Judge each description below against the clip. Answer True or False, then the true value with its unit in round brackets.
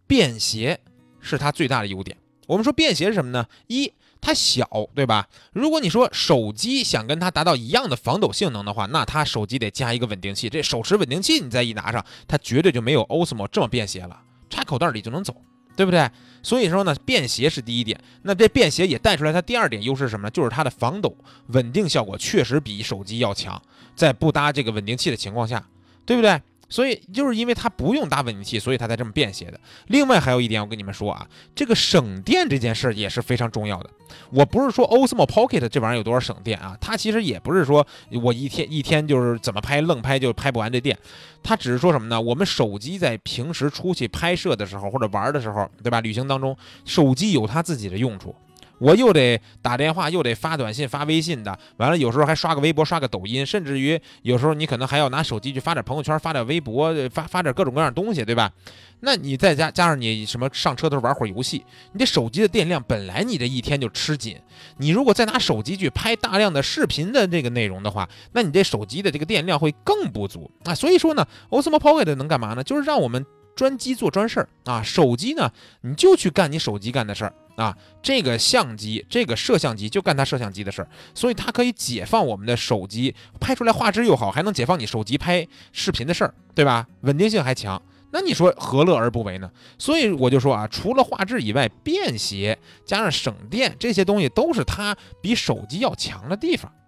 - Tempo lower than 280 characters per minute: False (350 characters per minute)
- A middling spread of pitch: False (7.6 semitones)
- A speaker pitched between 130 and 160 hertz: True (140 Hz)